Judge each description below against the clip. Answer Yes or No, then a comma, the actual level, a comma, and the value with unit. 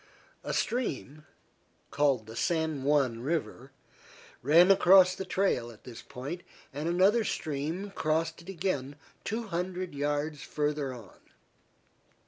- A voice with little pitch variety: No, average, 4.8 semitones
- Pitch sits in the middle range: Yes, medium, 155 Hz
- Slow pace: Yes, slow, 120 wpm